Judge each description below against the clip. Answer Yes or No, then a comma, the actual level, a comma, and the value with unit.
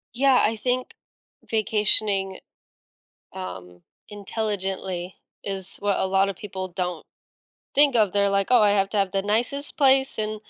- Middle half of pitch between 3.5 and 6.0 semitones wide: No, narrow, 2.5 semitones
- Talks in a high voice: Yes, high, 200 Hz